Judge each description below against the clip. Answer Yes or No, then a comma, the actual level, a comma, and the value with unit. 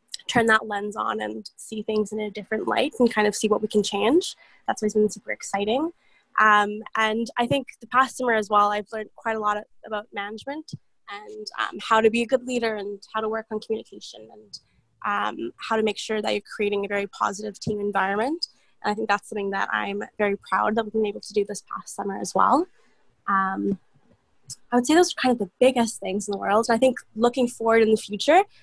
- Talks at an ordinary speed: No, fast, 230 wpm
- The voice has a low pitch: No, high, 215 Hz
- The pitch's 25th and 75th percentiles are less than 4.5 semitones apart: Yes, average, 2.7 semitones